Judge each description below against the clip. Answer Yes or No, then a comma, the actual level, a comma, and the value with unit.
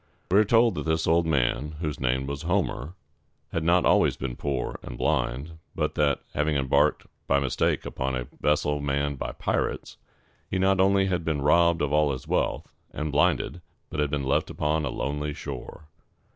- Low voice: Yes, very low, 75 Hz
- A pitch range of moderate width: Yes, average, 3.1 semitones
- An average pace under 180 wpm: No, average, 185 wpm